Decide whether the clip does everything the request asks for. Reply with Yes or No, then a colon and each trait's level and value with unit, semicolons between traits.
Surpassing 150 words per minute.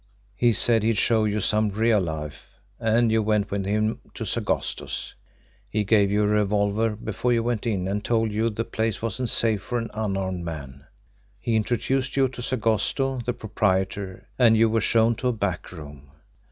Yes: average, 180 wpm